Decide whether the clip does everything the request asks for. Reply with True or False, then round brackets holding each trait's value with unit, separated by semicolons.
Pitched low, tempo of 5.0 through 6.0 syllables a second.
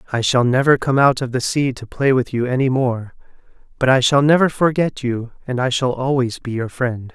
True (130 Hz; 5.2 syllables/s)